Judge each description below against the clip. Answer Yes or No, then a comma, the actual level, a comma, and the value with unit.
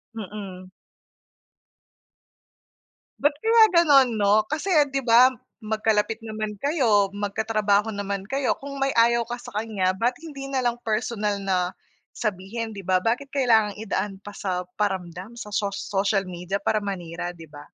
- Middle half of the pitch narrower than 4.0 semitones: Yes, average, 3.4 semitones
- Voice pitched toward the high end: Yes, high, 215 Hz